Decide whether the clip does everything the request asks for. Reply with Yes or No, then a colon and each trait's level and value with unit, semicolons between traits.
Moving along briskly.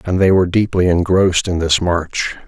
No: average, 195 wpm